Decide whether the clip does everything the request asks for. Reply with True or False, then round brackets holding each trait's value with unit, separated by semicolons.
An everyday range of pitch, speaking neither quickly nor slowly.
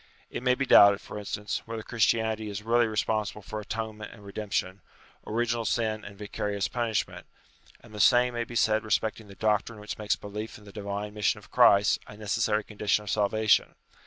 False (1.5 semitones; 190 wpm)